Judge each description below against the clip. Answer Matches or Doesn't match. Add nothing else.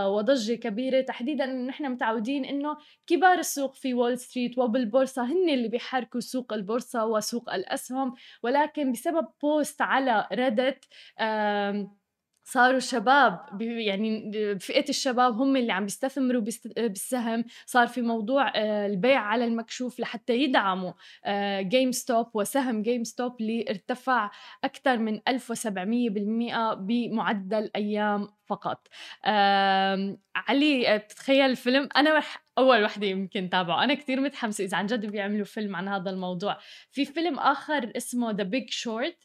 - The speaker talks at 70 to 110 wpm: Doesn't match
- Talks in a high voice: Matches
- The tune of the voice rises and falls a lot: Doesn't match